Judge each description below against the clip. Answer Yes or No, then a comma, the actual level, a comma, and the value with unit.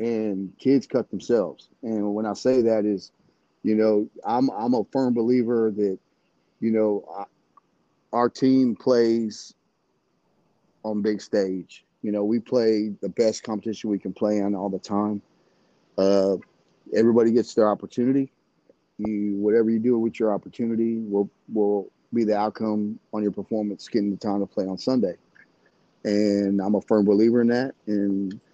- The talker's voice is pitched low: Yes, low, 105 Hz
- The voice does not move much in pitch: Yes, narrow, 2.1 semitones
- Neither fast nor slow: Yes, average, 160 wpm